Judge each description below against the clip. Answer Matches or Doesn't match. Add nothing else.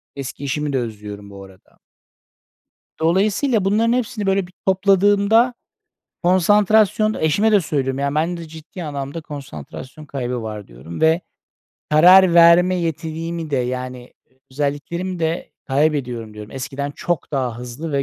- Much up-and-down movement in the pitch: Matches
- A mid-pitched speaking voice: Matches